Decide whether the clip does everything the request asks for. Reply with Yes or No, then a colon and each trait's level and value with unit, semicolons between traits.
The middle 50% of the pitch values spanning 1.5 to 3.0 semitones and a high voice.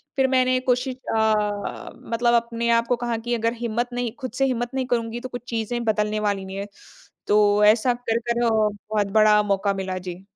Yes: narrow, 2.4 semitones; high, 230 Hz